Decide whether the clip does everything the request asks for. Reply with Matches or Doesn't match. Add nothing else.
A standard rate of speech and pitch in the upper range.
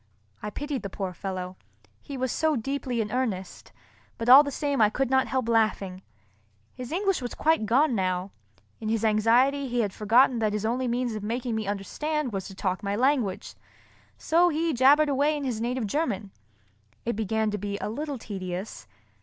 Matches